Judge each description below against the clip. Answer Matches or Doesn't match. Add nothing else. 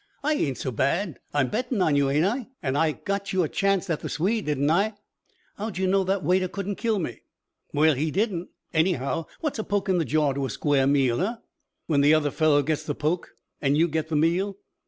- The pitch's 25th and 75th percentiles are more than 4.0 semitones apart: Matches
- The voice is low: Doesn't match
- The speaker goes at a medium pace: Doesn't match